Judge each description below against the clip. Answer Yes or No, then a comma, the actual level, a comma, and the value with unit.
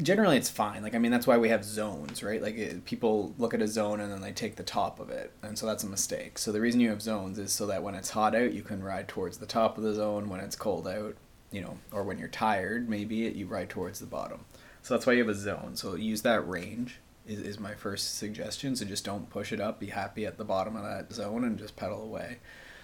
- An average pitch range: No, narrow, 1.7 semitones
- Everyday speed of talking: No, fast, 275 wpm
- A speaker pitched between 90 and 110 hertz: Yes, low, 105 Hz